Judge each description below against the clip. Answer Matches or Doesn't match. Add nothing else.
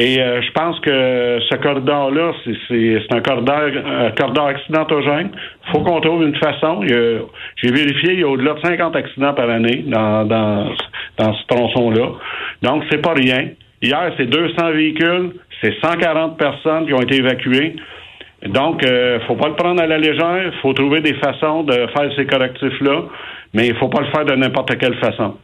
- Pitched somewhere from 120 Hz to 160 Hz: Matches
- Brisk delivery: Doesn't match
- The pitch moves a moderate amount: Matches